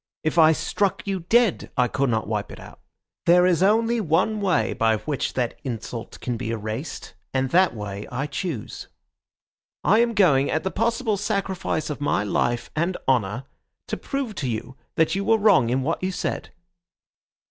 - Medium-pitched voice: Yes, medium, 155 Hz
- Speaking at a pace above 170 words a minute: Yes, average, 180 wpm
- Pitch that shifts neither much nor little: No, wide, 8.2 semitones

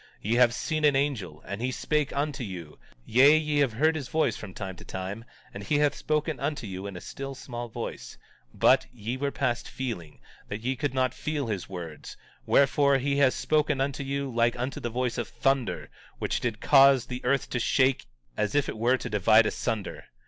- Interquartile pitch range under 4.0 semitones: No, average, 4.3 semitones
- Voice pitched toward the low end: Yes, low, 125 Hz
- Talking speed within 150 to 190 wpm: No, fast, 205 wpm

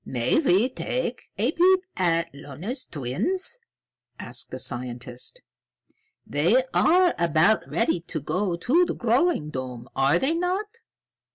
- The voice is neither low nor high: No, high, 200 Hz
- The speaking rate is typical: No, slow, 125 wpm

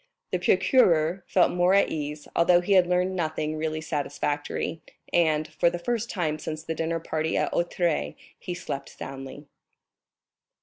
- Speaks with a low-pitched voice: No, medium, 165 Hz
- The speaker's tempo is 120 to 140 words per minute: No, average, 150 wpm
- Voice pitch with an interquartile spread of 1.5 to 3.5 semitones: Yes, narrow, 2.5 semitones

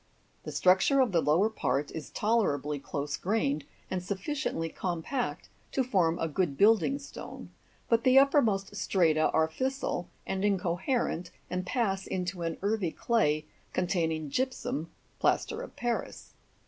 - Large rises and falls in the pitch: Yes, wide, 6.0 semitones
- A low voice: No, medium, 185 Hz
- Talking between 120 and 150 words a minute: Yes, slow, 135 wpm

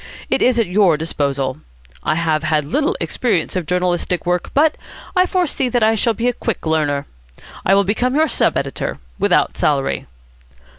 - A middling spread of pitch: No, wide, 7.6 semitones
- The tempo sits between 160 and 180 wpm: Yes, average, 170 wpm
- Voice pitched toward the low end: No, medium, 180 Hz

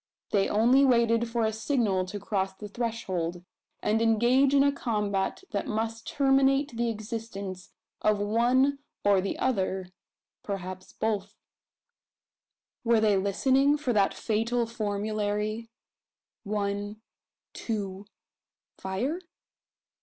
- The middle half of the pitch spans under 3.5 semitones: Yes, average, 2.9 semitones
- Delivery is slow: Yes, slow, 110 wpm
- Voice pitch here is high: Yes, high, 220 Hz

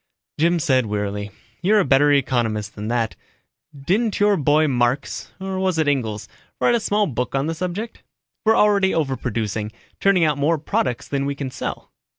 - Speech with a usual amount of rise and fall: No, wide, 7.5 semitones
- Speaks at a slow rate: No, average, 170 wpm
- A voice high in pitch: No, medium, 145 Hz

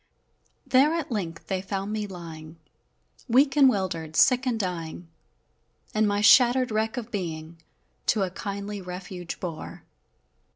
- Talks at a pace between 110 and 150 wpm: Yes, slow, 135 wpm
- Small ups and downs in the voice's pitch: No, average, 5.3 semitones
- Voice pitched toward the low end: No, high, 200 Hz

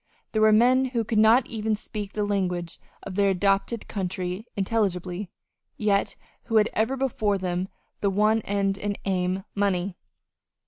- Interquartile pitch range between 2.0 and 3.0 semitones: Yes, narrow, 2.5 semitones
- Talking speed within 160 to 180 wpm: No, average, 150 wpm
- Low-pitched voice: No, high, 205 Hz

